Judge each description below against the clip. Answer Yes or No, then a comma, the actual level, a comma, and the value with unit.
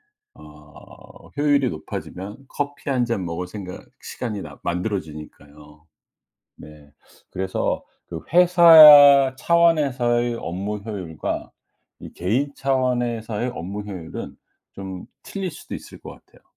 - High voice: No, low, 105 Hz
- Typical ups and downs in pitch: No, wide, 7.7 semitones